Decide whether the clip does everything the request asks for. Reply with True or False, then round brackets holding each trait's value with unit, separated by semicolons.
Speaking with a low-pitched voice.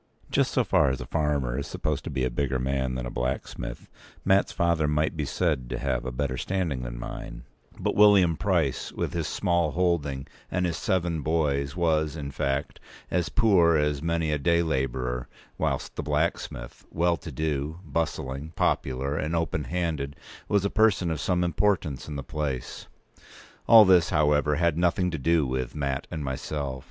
True (75 Hz)